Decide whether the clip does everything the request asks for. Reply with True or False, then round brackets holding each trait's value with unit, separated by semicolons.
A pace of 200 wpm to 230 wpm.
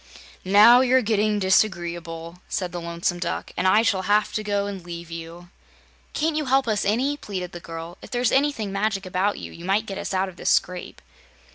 True (205 wpm)